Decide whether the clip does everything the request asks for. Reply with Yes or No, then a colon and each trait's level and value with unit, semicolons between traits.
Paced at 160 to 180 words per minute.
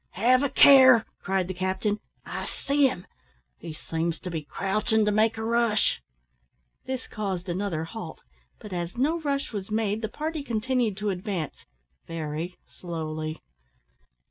No: average, 145 wpm